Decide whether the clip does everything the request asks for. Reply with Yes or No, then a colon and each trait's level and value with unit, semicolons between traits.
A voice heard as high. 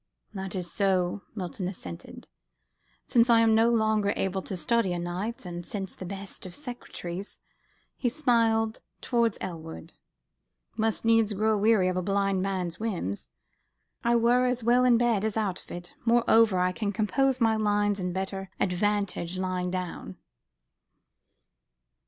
Yes: high, 200 Hz